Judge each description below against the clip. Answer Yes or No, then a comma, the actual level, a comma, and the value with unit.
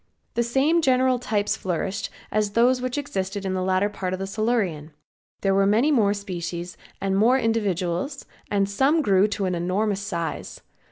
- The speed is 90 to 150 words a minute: No, average, 165 wpm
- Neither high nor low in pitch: No, high, 200 Hz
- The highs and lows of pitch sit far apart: No, average, 4.0 semitones